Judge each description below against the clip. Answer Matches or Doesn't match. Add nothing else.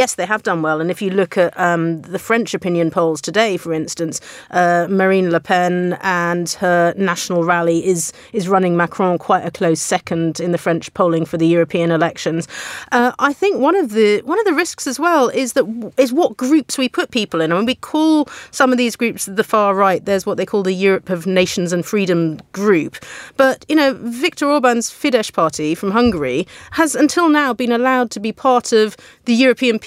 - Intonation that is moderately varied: Doesn't match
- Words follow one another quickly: Matches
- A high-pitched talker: Matches